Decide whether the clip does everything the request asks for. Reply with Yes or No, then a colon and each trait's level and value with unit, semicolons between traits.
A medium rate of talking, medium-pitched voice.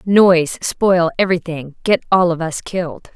Yes: average, 150 wpm; medium, 175 Hz